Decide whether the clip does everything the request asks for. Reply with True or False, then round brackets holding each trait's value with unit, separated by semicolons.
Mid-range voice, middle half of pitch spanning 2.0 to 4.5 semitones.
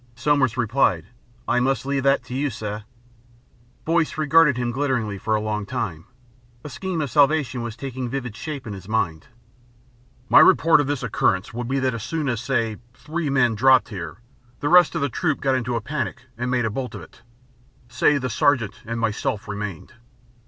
False (125 Hz; 4.1 semitones)